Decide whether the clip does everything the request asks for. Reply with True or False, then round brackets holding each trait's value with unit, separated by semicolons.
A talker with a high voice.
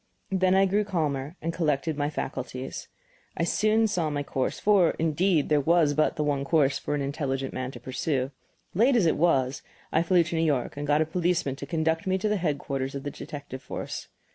False (155 Hz)